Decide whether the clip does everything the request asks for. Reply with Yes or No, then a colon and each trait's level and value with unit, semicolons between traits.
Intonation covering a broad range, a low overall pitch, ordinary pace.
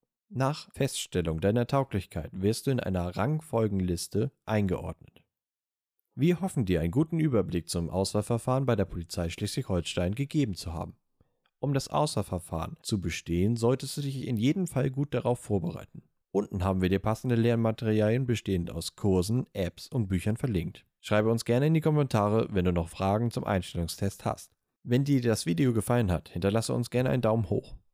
Yes: wide, 5.7 semitones; low, 110 Hz; average, 165 wpm